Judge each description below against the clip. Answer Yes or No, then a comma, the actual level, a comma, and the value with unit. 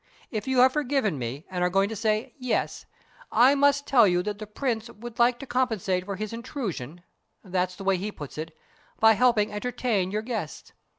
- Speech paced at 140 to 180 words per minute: No, average, 195 wpm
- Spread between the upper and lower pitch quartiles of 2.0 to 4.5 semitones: No, average, 4.9 semitones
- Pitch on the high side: Yes, high, 215 Hz